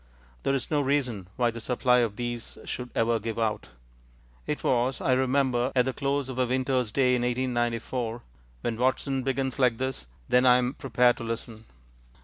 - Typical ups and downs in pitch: No, narrow, 1.9 semitones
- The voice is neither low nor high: No, low, 125 Hz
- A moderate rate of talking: Yes, average, 180 wpm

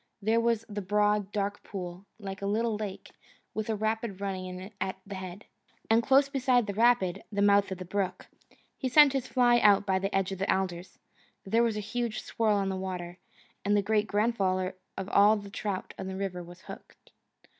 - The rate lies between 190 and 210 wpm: Yes, fast, 205 wpm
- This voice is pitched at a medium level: No, high, 200 Hz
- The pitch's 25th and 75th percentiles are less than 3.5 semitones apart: Yes, narrow, 2.6 semitones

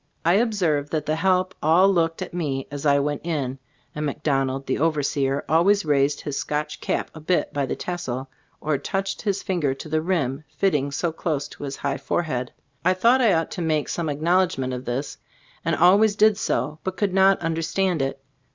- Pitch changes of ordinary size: Yes, average, 4.5 semitones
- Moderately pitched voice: Yes, medium, 155 Hz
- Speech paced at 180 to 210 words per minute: Yes, average, 195 wpm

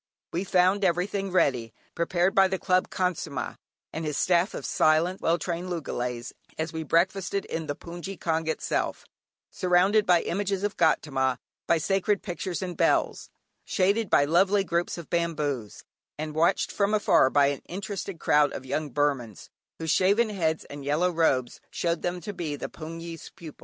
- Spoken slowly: No, average, 165 wpm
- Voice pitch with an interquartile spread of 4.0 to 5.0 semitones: No, average, 3.6 semitones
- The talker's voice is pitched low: No, medium, 170 Hz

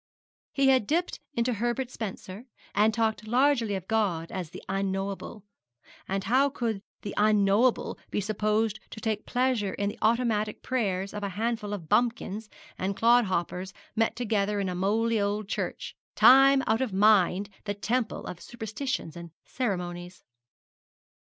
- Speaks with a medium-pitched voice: No, high, 215 Hz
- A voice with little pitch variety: No, average, 3.2 semitones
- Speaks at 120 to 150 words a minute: Yes, average, 145 wpm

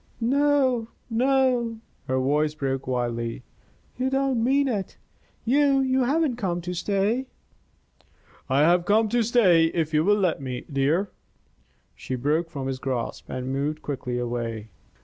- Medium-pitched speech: Yes, medium, 175 Hz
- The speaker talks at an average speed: Yes, average, 145 wpm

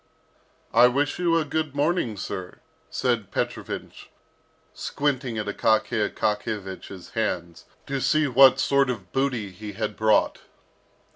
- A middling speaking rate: No, slow, 125 wpm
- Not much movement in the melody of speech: No, average, 5.1 semitones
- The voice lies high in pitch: No, low, 120 Hz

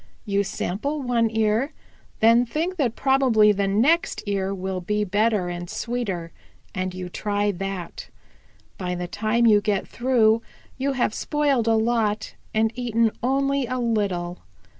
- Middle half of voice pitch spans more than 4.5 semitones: No, average, 3.8 semitones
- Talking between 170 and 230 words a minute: No, average, 145 wpm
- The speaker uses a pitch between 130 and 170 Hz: No, high, 220 Hz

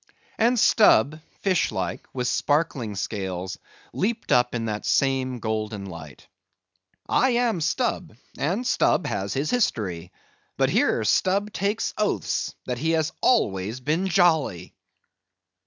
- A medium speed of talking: No, slow, 125 wpm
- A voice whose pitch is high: No, medium, 140 Hz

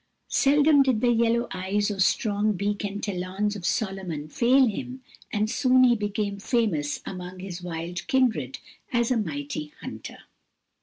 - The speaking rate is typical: Yes, average, 150 wpm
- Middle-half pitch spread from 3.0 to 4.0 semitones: No, average, 4.6 semitones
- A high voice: Yes, high, 205 Hz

